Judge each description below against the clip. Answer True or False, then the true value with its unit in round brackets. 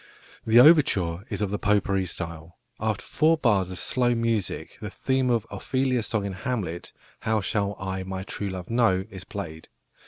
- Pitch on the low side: True (100 Hz)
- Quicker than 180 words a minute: False (175 wpm)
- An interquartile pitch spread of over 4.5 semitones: False (4.1 semitones)